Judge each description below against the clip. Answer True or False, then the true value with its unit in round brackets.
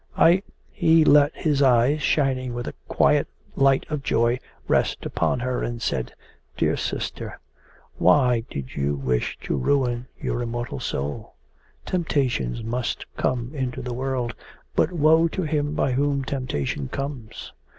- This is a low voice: True (130 Hz)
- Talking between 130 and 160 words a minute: True (140 wpm)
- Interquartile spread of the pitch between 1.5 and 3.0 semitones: False (3.5 semitones)